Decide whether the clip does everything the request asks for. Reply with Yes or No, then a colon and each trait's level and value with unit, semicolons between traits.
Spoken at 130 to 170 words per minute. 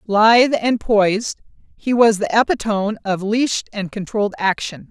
Yes: average, 145 wpm